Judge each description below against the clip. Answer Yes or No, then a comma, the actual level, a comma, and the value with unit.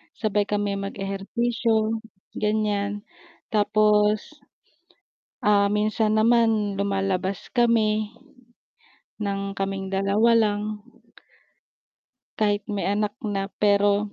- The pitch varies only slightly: Yes, narrow, 1.3 semitones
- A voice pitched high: Yes, high, 210 Hz